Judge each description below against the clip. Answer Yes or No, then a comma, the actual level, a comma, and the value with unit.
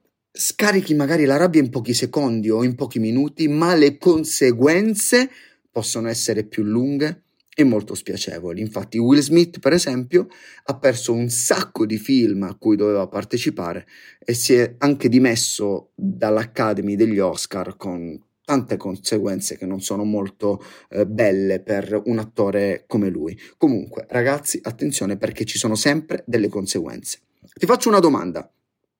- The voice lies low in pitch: Yes, low, 120 Hz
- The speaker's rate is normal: Yes, average, 145 wpm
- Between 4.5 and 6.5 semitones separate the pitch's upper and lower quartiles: Yes, wide, 5.6 semitones